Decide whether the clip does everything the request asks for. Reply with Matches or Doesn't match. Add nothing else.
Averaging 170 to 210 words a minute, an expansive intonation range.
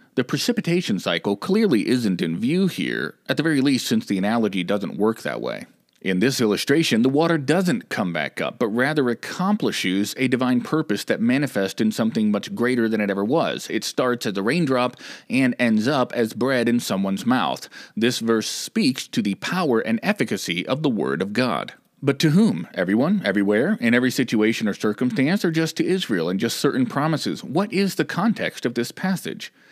Matches